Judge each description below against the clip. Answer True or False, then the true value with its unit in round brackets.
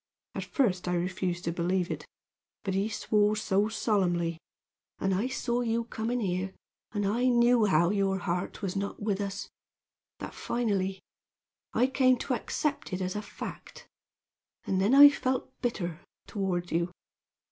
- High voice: True (200 Hz)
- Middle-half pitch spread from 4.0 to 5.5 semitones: True (4.3 semitones)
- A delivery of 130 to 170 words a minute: True (155 wpm)